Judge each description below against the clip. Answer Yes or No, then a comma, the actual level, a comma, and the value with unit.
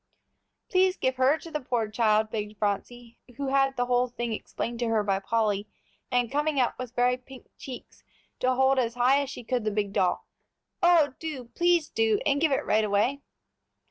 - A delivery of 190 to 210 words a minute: Yes, average, 195 wpm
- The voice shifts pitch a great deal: No, average, 3.7 semitones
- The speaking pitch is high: Yes, high, 245 Hz